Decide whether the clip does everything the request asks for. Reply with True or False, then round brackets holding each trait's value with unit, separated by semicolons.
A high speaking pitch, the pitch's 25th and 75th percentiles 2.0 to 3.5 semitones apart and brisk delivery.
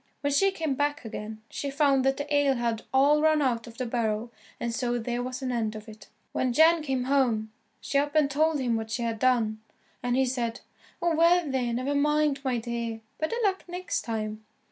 False (255 Hz; 3.9 semitones; 210 wpm)